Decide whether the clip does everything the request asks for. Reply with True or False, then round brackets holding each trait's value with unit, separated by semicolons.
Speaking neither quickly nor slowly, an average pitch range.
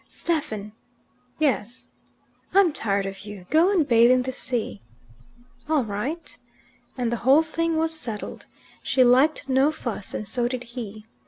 False (150 wpm; 6.2 semitones)